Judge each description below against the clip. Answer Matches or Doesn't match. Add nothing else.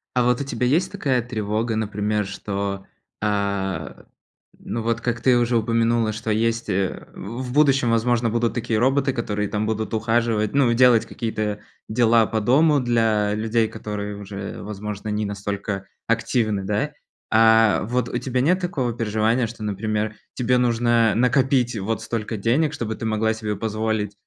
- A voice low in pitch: Matches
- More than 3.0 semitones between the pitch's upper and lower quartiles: Doesn't match